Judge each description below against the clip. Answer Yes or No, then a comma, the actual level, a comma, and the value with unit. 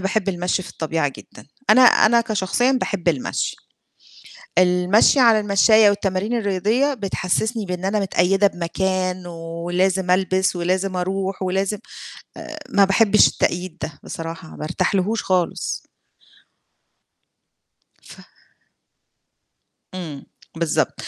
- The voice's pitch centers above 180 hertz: Yes, high, 190 Hz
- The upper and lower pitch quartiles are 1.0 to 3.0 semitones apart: Yes, narrow, 2.4 semitones